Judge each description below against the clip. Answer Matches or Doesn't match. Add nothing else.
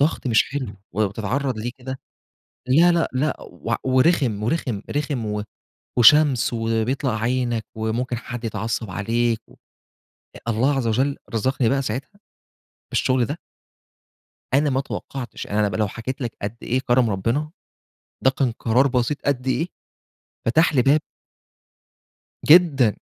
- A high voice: Doesn't match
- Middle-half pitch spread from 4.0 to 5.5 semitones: Doesn't match